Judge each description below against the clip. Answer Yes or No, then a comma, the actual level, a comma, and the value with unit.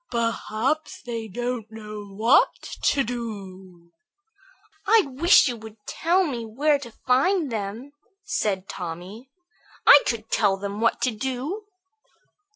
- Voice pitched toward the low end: No, high, 230 Hz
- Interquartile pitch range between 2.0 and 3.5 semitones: No, average, 4.4 semitones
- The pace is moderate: No, slow, 125 wpm